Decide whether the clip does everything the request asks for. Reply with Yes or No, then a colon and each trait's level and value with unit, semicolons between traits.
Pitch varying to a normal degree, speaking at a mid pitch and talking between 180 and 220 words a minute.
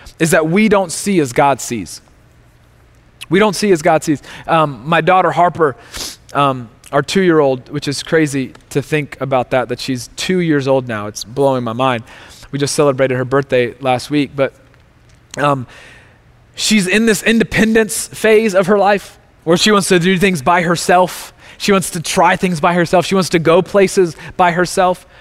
No: wide, 5.8 semitones; medium, 155 Hz; average, 190 wpm